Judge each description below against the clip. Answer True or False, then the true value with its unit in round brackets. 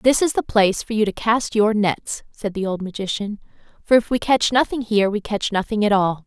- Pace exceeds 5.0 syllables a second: True (5.4 syllables/s)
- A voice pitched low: False (210 Hz)